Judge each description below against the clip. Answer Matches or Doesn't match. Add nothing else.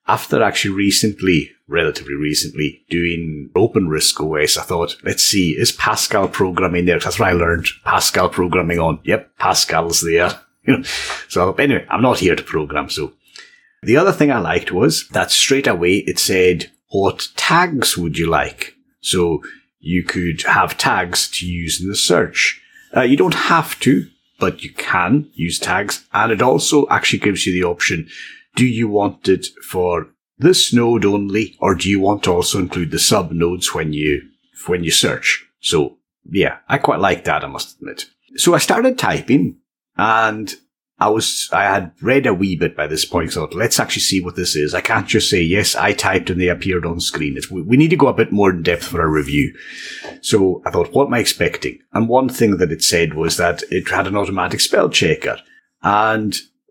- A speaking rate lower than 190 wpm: Doesn't match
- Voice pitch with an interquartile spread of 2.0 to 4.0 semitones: Matches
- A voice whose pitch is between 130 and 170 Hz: Doesn't match